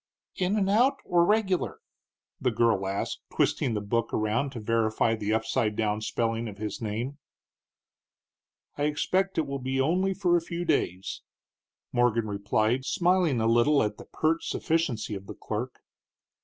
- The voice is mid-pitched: No, low, 120 Hz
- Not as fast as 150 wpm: No, average, 155 wpm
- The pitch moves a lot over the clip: Yes, wide, 7.3 semitones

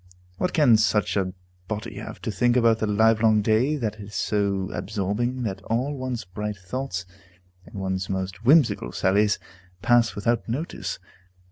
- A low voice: Yes, low, 110 Hz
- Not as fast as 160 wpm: Yes, average, 150 wpm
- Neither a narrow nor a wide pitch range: Yes, average, 3.3 semitones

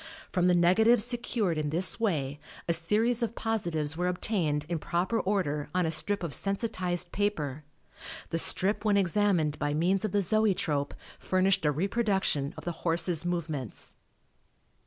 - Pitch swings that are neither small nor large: Yes, average, 4.5 semitones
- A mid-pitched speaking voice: Yes, medium, 180 Hz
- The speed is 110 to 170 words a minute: Yes, average, 155 wpm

